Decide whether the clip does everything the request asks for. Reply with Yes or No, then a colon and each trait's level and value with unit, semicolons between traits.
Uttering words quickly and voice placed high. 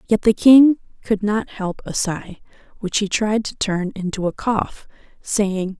No: average, 175 wpm; high, 205 Hz